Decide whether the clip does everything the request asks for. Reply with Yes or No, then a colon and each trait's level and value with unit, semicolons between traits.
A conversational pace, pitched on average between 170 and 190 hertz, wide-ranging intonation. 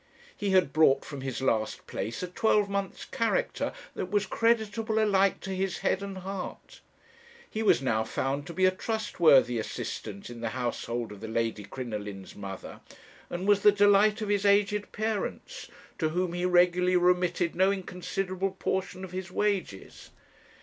Yes: average, 160 wpm; medium, 185 Hz; wide, 7.0 semitones